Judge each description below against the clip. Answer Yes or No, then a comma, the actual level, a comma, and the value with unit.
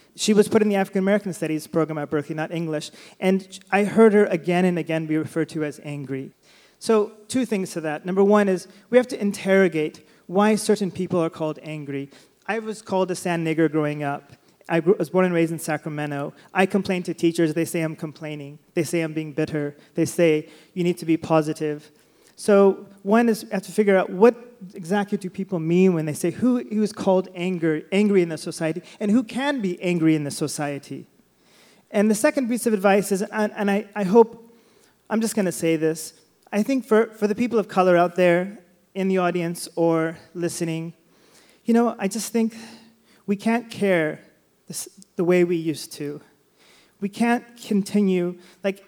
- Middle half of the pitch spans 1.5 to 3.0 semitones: No, average, 4.3 semitones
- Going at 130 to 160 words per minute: No, average, 200 wpm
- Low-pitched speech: No, medium, 185 Hz